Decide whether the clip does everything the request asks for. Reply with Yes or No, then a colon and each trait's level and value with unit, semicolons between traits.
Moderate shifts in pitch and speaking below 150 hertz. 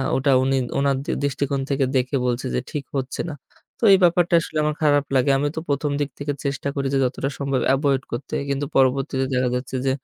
No: narrow, 1.4 semitones; medium, 140 Hz